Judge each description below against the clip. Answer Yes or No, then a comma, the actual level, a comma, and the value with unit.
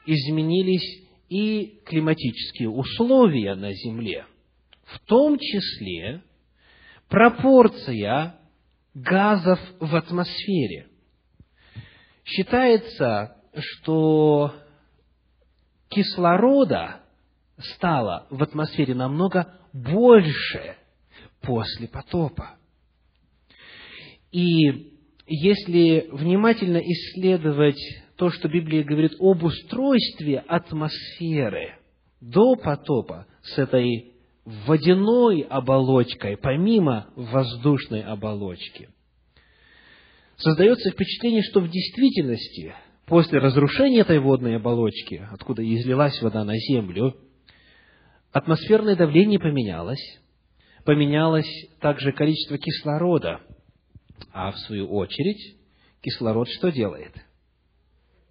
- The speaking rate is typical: No, slow, 75 wpm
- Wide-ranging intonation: Yes, wide, 7.6 semitones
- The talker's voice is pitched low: No, medium, 150 Hz